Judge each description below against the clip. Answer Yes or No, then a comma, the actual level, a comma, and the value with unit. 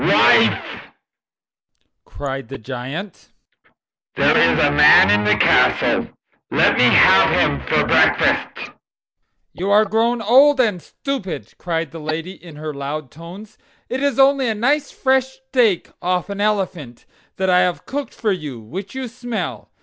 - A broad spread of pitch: Yes, wide, 8.0 semitones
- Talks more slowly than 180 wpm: Yes, average, 150 wpm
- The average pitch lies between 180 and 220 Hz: Yes, high, 190 Hz